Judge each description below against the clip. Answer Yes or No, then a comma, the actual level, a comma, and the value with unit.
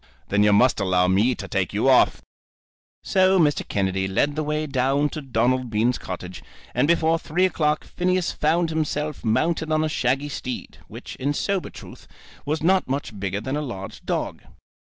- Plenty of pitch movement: Yes, wide, 6.8 semitones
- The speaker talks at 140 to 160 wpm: No, average, 175 wpm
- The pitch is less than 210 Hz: Yes, medium, 140 Hz